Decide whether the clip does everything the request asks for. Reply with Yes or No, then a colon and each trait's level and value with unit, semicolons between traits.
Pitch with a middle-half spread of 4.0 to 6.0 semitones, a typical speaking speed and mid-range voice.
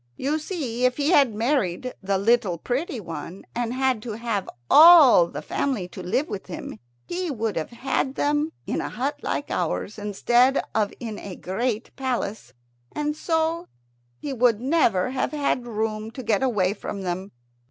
No: average, 5.2 semitones; average, 170 wpm; high, 240 Hz